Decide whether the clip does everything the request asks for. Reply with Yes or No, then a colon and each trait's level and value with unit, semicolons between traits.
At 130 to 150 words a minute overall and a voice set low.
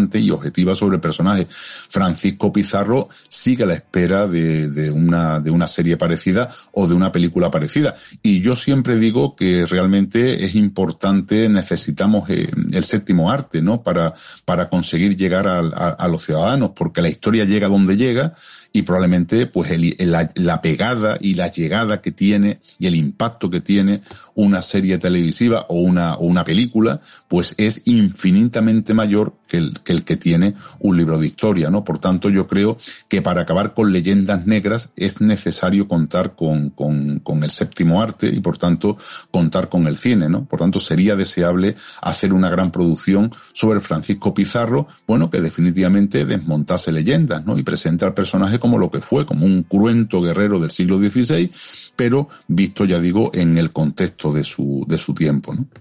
No: average, 175 wpm; very low, 95 Hz